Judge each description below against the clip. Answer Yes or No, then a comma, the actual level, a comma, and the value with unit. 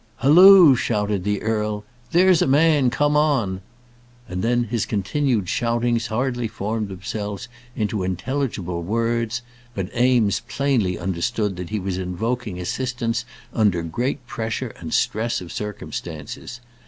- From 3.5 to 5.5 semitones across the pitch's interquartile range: Yes, average, 4.0 semitones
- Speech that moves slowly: Yes, slow, 130 wpm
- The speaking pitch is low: Yes, low, 110 Hz